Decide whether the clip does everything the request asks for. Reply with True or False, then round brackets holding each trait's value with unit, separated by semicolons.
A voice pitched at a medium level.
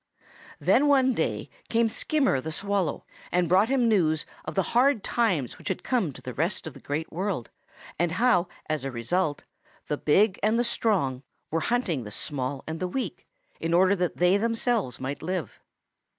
True (180 Hz)